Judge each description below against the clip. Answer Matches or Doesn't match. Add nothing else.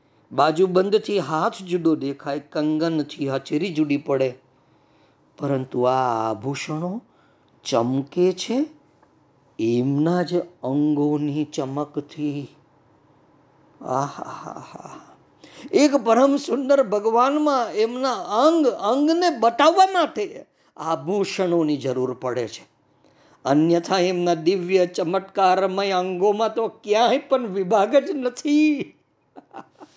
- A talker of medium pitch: Matches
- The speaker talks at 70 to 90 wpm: Matches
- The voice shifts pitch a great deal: Matches